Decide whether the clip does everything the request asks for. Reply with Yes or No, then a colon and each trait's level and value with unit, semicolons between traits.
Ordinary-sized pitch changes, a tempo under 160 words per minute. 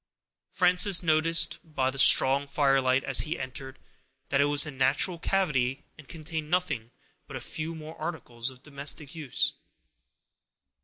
Yes: average, 3.5 semitones; average, 145 wpm